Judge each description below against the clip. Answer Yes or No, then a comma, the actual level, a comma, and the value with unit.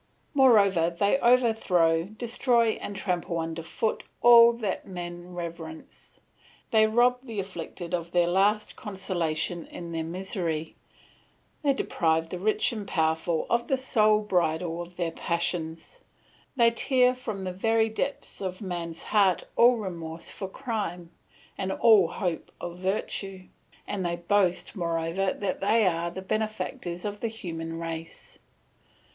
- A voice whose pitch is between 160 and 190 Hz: Yes, medium, 185 Hz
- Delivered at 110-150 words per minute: Yes, average, 140 wpm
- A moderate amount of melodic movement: Yes, average, 4.3 semitones